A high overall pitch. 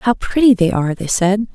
Yes: high, 205 Hz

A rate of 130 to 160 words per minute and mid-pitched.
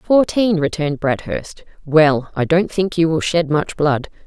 No: average, 170 wpm; medium, 165 Hz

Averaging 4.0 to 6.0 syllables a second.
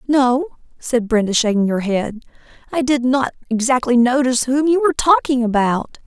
Yes: 5.1 syllables/s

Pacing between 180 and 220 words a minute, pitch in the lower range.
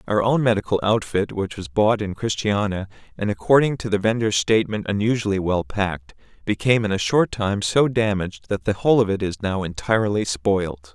Yes: average, 185 wpm; low, 105 Hz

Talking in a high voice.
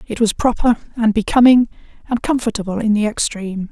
Yes: high, 220 Hz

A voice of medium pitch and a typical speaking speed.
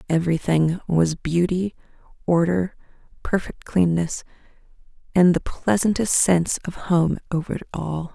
No: medium, 170 Hz; slow, 110 wpm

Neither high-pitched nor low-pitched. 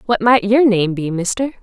No: high, 215 Hz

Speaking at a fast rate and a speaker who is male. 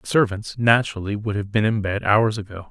Yes: fast, 220 wpm; male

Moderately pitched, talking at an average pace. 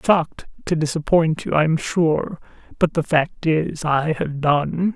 Yes: medium, 160 Hz; average, 170 wpm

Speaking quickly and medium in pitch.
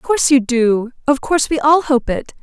No: fast, 245 wpm; very high, 270 Hz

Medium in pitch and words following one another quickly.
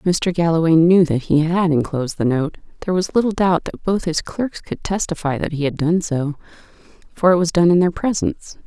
Yes: medium, 170 Hz; fast, 215 wpm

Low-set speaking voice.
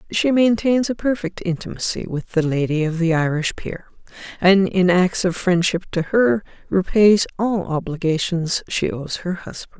No: medium, 180 Hz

